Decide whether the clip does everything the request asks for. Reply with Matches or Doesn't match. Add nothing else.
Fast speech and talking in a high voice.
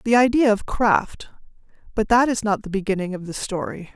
Doesn't match